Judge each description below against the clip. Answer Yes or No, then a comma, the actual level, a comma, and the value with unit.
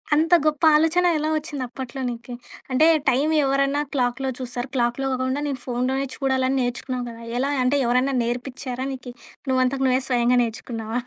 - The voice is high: Yes, very high, 260 Hz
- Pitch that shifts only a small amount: Yes, narrow, 2.1 semitones